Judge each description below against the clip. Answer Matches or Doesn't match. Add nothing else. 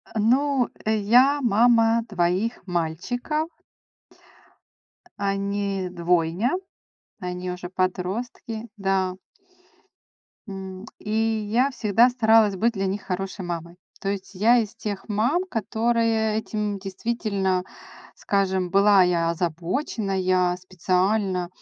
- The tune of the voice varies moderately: Matches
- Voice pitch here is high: Matches